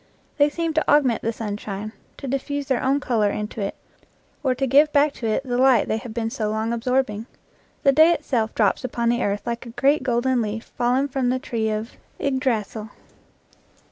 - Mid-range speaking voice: No, high, 245 Hz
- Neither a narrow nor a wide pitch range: Yes, average, 3.6 semitones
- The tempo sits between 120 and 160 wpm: No, average, 195 wpm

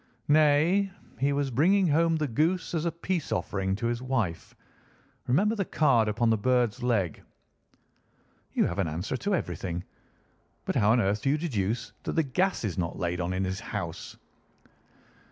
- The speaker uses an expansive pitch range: Yes, wide, 8.2 semitones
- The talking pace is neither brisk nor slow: Yes, average, 170 wpm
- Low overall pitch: Yes, low, 125 Hz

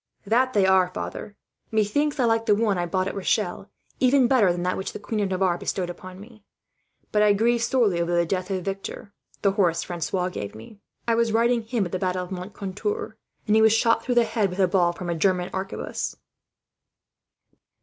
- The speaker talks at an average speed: No, fast, 210 wpm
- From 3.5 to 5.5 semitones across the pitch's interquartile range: Yes, average, 3.8 semitones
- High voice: Yes, high, 195 Hz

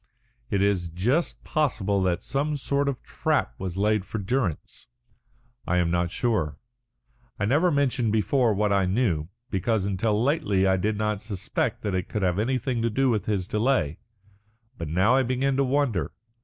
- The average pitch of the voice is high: No, low, 105 Hz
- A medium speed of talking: Yes, average, 170 wpm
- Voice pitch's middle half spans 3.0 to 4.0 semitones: No, wide, 5.5 semitones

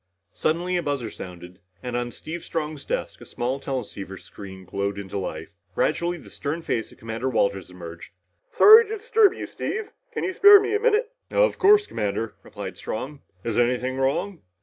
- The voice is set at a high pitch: No, low, 130 Hz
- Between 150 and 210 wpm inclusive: Yes, average, 175 wpm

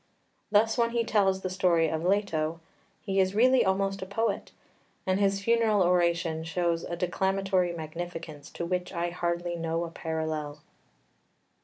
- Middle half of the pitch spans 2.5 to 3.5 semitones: Yes, average, 2.9 semitones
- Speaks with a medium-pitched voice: Yes, medium, 180 Hz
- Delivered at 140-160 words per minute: Yes, average, 150 wpm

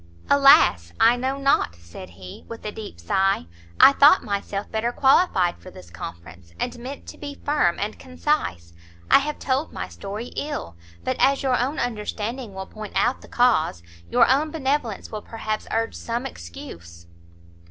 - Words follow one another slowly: No, average, 165 wpm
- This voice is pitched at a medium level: No, high, 225 Hz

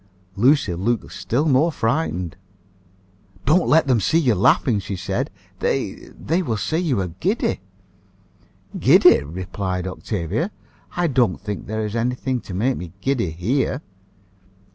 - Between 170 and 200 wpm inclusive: No, average, 140 wpm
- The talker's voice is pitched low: Yes, low, 115 Hz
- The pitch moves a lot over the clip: Yes, wide, 6.9 semitones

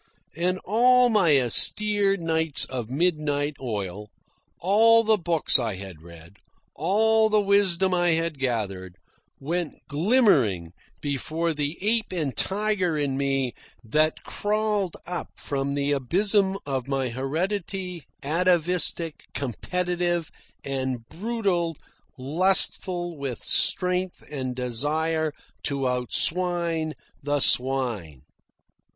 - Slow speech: Yes, slow, 105 wpm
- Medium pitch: Yes, medium, 160 Hz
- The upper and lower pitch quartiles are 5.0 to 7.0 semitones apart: Yes, wide, 5.6 semitones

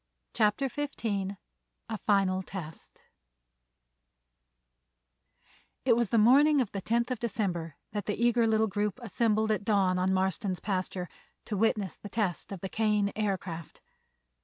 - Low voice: No, high, 205 Hz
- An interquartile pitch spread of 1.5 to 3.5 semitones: Yes, average, 3.0 semitones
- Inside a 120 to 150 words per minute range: Yes, slow, 135 wpm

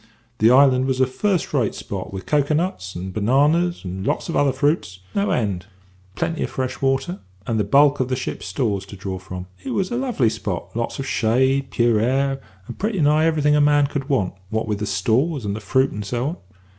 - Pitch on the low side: Yes, low, 130 Hz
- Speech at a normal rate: No, fast, 220 wpm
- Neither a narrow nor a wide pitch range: No, wide, 5.7 semitones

